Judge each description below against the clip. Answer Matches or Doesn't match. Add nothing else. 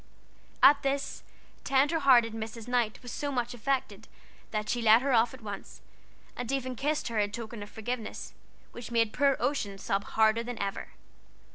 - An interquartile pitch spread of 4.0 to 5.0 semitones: Doesn't match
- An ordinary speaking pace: Matches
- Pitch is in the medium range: Doesn't match